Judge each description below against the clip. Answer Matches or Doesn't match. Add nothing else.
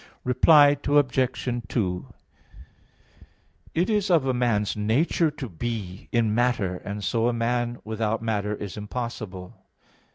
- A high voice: Doesn't match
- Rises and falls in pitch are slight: Doesn't match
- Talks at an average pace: Doesn't match